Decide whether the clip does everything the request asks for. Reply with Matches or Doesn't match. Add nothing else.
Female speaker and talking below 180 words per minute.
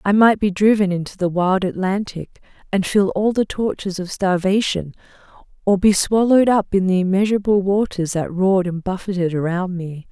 Matches